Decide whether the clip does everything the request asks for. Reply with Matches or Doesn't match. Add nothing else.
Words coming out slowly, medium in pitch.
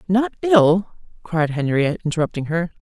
Matches